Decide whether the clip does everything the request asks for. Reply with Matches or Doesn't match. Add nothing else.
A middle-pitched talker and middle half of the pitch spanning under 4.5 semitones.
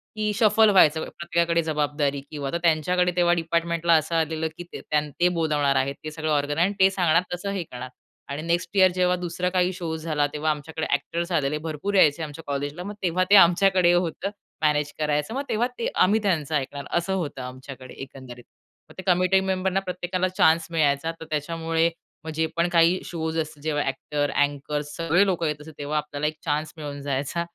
Matches